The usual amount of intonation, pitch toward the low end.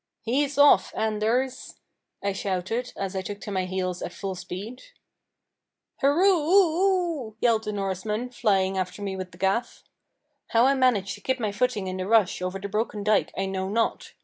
No: average, 4.8 semitones; high, 210 Hz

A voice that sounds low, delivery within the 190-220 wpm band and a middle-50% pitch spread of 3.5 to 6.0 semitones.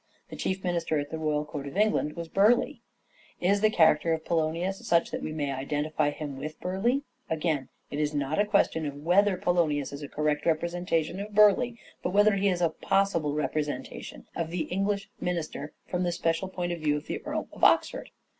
No: medium, 165 Hz; average, 200 wpm; average, 4.0 semitones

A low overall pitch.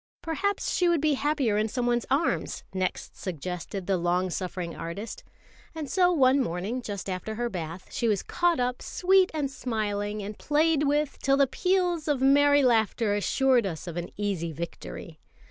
No: high, 240 Hz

